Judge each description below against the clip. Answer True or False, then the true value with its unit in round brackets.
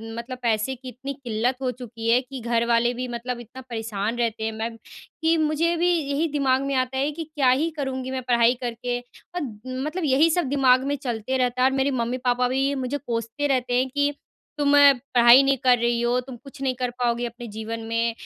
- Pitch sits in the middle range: False (255 Hz)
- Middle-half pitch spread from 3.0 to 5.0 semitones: False (2.5 semitones)